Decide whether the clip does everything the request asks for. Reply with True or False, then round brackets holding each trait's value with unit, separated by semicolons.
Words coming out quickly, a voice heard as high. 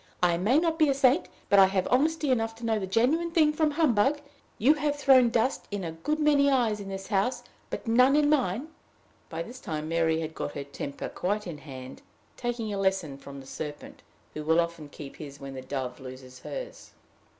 True (210 wpm; 205 Hz)